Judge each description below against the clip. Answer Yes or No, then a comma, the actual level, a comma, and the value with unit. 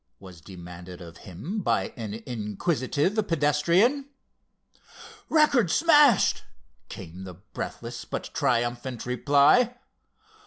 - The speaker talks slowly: Yes, slow, 90 wpm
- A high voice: No, low, 125 Hz